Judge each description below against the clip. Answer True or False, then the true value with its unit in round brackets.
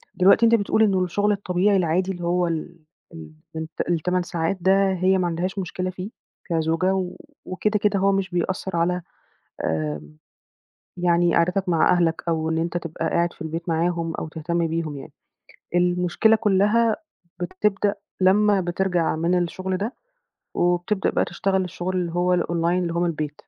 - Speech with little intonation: True (2.2 semitones)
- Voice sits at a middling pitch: True (180 Hz)